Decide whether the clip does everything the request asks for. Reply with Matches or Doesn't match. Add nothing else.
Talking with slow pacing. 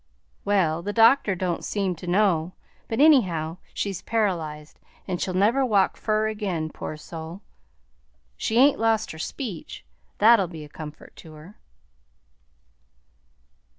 Matches